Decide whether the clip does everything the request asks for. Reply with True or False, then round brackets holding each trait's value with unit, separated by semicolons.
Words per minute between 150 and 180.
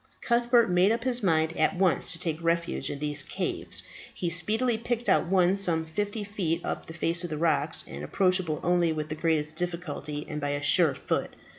False (200 wpm)